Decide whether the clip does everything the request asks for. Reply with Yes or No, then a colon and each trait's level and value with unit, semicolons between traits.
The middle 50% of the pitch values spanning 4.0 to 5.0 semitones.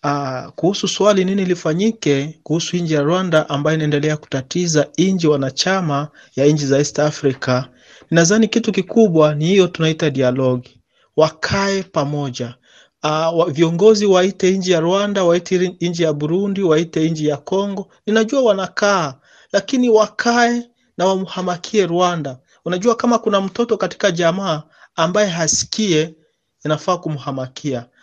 Yes: average, 4.5 semitones